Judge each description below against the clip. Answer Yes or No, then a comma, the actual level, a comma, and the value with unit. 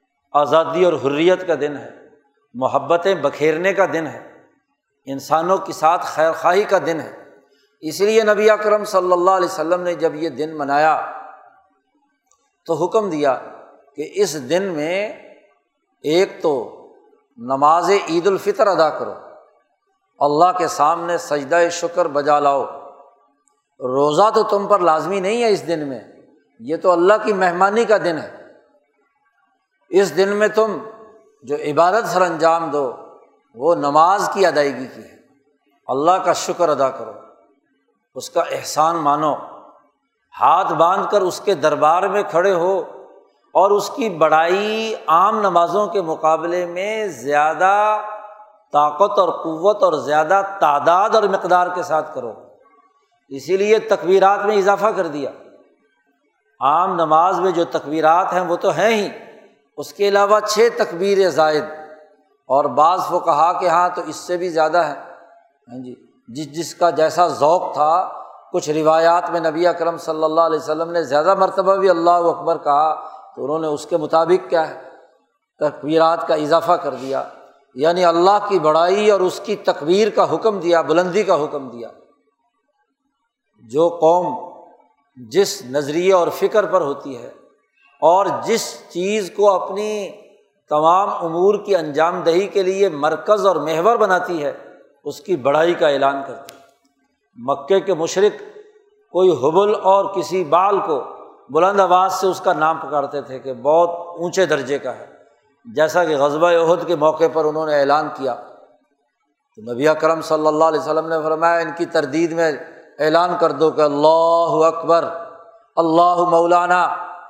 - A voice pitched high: No, medium, 175 Hz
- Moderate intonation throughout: Yes, average, 4.3 semitones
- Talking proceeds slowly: No, average, 155 wpm